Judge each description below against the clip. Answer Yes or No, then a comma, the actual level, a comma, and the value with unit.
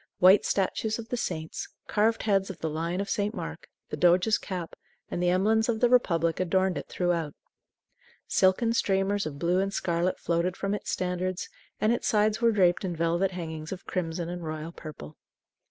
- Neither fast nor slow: Yes, average, 185 wpm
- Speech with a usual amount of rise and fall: Yes, average, 3.3 semitones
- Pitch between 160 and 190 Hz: Yes, medium, 185 Hz